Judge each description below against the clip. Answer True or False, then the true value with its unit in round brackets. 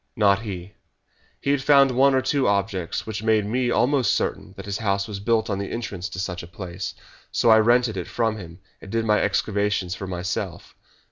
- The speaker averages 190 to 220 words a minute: True (205 wpm)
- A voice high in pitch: False (105 Hz)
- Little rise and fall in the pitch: False (3.4 semitones)